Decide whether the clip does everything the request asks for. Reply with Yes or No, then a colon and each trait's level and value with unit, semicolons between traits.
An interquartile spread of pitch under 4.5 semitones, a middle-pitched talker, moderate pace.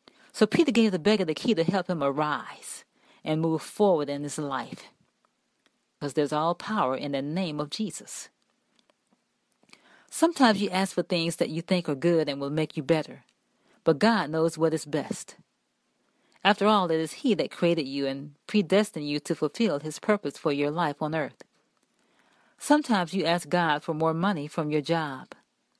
No: average, 5.2 semitones; medium, 165 Hz; average, 180 wpm